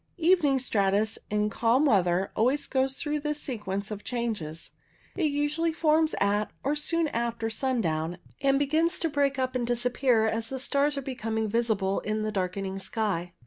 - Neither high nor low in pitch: No, high, 235 Hz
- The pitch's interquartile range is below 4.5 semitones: No, wide, 5.4 semitones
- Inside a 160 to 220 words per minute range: Yes, average, 170 wpm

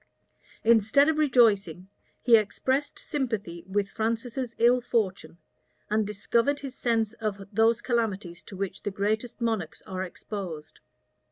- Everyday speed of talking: No, slow, 125 wpm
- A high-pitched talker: Yes, high, 220 Hz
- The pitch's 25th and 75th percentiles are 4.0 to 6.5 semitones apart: No, average, 3.3 semitones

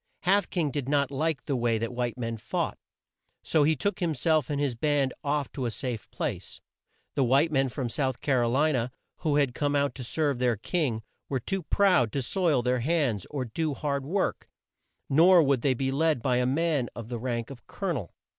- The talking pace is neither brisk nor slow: No, fast, 220 wpm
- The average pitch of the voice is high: No, medium, 140 Hz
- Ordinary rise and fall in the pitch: Yes, average, 4.0 semitones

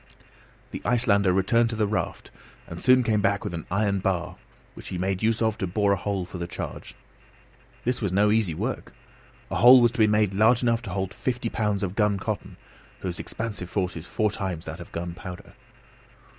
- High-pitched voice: No, low, 100 Hz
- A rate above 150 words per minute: Yes, average, 200 wpm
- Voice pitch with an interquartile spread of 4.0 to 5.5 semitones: No, average, 3.4 semitones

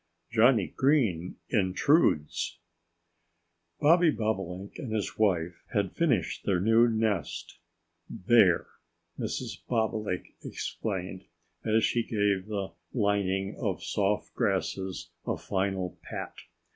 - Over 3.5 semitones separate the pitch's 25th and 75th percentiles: No, average, 3.2 semitones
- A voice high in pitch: No, low, 100 Hz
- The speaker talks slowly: Yes, slow, 105 wpm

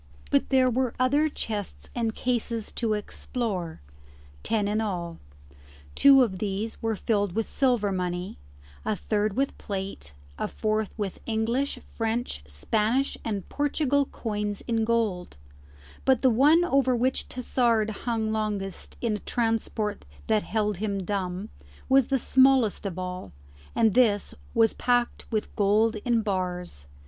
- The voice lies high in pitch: Yes, high, 220 Hz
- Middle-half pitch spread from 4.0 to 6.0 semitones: No, average, 3.2 semitones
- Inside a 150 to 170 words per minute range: No, average, 140 wpm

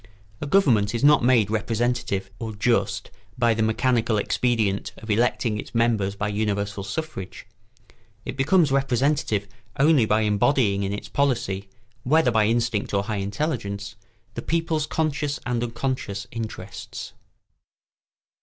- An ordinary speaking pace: No, slow, 130 wpm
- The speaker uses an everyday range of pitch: Yes, average, 4.4 semitones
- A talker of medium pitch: No, low, 115 Hz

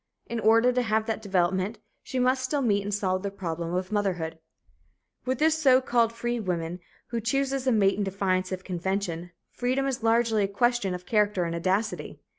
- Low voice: No, high, 210 Hz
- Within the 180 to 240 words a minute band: Yes, average, 190 wpm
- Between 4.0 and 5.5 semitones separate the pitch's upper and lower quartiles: Yes, average, 4.4 semitones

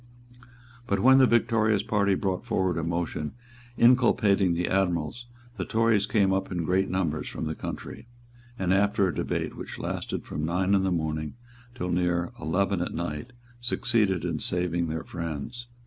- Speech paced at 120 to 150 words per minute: No, average, 165 wpm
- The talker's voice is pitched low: Yes, very low, 95 Hz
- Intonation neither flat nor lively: Yes, average, 3.7 semitones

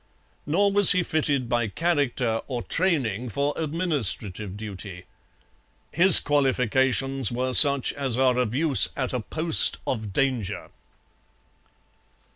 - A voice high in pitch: No, low, 130 Hz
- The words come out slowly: Yes, slow, 115 wpm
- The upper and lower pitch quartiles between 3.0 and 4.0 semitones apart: No, average, 4.6 semitones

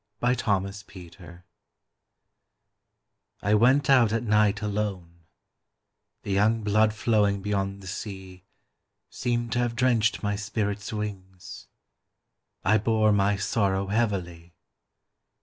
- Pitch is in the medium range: No, low, 105 Hz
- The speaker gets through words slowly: Yes, slow, 105 wpm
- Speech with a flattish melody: Yes, narrow, 2.2 semitones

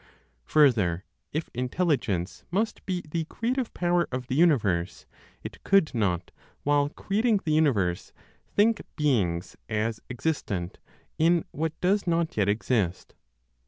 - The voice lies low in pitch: No, medium, 145 Hz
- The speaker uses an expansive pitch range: Yes, wide, 8.8 semitones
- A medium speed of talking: No, slow, 125 wpm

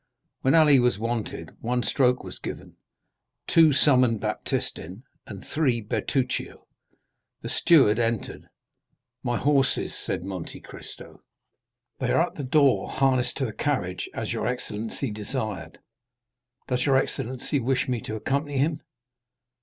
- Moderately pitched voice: No, low, 125 Hz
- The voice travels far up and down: No, average, 3.6 semitones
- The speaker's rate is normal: No, slow, 130 wpm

